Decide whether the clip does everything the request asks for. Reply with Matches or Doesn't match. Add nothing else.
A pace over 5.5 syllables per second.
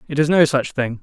Matches